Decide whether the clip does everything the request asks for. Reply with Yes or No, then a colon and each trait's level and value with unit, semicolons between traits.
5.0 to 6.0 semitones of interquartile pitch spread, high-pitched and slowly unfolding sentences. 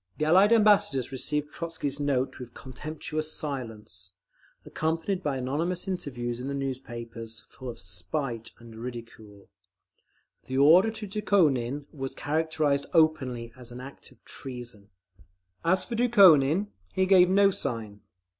No: wide, 5.4 semitones; medium, 140 Hz; slow, 130 wpm